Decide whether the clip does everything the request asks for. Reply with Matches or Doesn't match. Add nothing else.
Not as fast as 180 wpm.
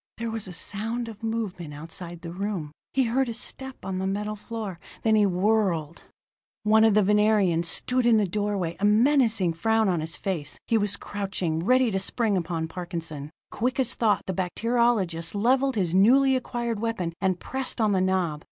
Doesn't match